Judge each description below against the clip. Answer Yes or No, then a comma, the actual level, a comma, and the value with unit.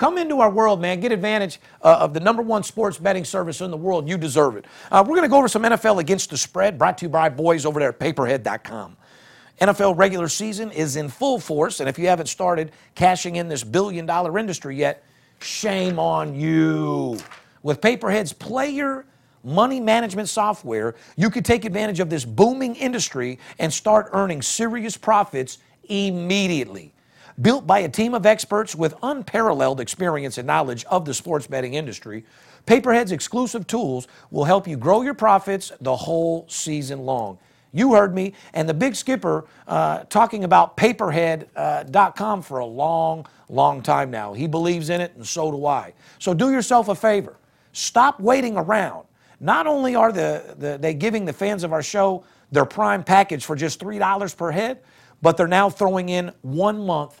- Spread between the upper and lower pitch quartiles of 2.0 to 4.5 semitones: No, wide, 5.6 semitones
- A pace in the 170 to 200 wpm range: Yes, average, 185 wpm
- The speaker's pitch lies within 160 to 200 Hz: Yes, medium, 185 Hz